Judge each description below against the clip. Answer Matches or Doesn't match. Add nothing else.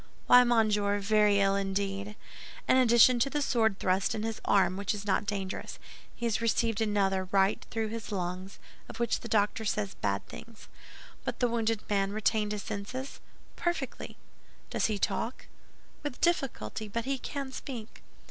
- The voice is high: Matches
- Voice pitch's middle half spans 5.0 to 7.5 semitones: Doesn't match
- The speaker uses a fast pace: Doesn't match